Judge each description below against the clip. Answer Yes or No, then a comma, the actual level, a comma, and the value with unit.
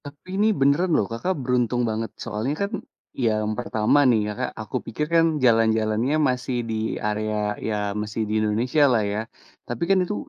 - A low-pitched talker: Yes, low, 115 Hz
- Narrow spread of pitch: No, average, 4.4 semitones